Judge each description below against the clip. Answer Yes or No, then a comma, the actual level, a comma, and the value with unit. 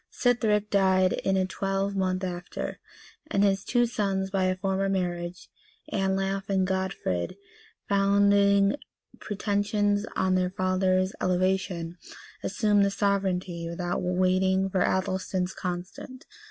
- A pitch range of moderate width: No, narrow, 1.3 semitones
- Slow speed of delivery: Yes, slow, 115 wpm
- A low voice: No, high, 190 Hz